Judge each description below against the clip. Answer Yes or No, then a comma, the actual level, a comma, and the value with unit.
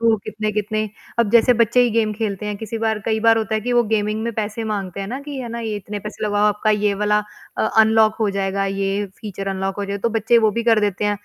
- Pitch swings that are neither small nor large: No, narrow, 1.7 semitones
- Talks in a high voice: Yes, high, 215 Hz